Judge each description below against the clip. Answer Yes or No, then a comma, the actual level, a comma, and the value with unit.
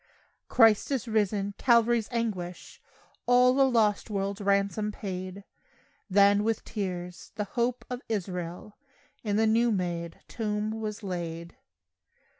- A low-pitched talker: No, high, 210 Hz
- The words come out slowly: Yes, slow, 120 wpm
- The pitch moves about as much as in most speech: Yes, average, 3.3 semitones